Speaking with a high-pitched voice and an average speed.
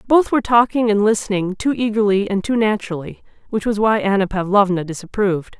Yes: high, 205 Hz; average, 170 wpm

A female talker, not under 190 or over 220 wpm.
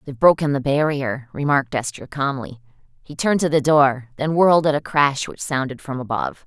Yes: female; average, 195 wpm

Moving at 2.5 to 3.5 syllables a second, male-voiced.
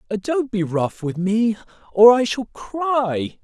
Yes: 3.2 syllables/s; male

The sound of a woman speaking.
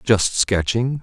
No: male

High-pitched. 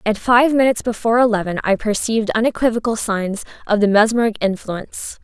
Yes: high, 220 Hz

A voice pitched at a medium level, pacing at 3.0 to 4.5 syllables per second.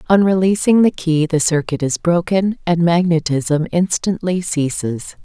Yes: medium, 170 Hz; 4.2 syllables/s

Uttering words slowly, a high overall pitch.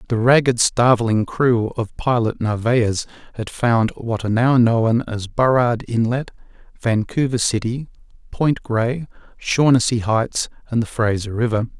No: slow, 130 wpm; low, 120 Hz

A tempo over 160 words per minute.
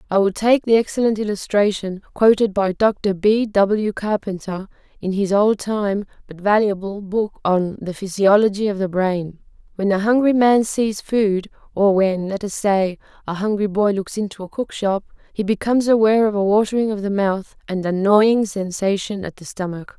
Yes: average, 175 wpm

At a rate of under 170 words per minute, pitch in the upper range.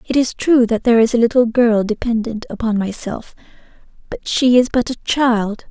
No: average, 190 wpm; high, 235 Hz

